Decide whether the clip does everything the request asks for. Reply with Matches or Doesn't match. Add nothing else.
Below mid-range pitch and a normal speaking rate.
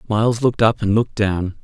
Doesn't match